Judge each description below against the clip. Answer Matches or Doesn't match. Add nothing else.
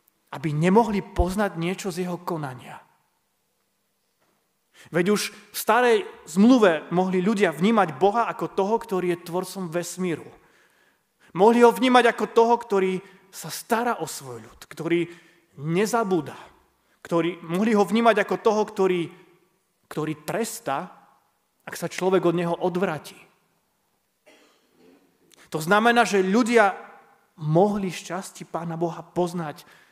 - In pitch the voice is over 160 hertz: Matches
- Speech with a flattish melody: Doesn't match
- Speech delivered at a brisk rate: Doesn't match